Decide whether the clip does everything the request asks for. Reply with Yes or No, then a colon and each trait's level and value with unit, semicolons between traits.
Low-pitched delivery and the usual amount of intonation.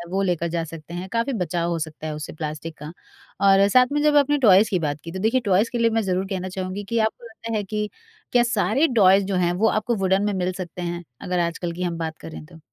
No: medium, 185 Hz; average, 4.2 semitones